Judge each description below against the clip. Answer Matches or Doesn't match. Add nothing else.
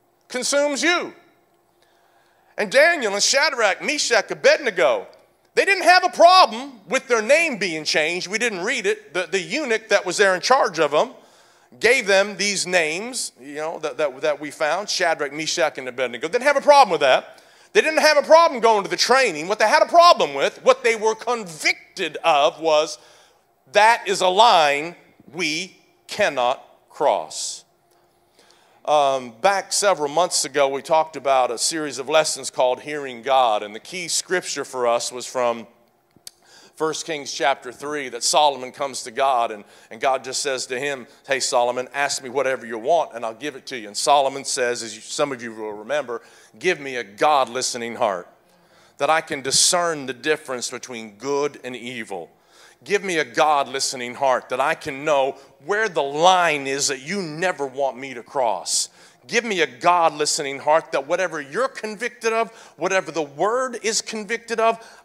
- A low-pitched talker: Doesn't match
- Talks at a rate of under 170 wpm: Doesn't match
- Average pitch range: Doesn't match